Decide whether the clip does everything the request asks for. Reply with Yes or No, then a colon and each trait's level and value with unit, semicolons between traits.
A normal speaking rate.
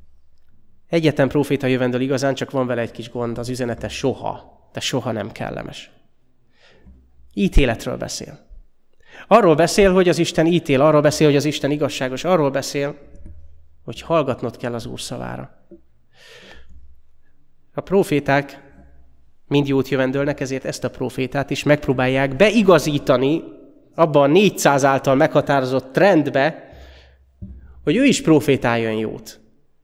Yes: average, 125 wpm